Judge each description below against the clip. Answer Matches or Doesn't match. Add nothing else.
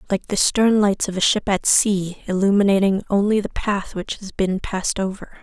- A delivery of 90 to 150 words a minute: Doesn't match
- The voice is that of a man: Doesn't match